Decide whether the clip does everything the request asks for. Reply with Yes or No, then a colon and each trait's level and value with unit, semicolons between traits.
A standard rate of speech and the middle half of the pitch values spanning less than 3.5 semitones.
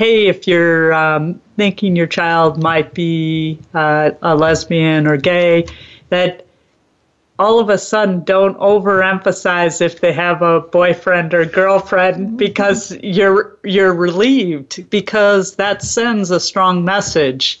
No: slow, 130 wpm; average, 3.1 semitones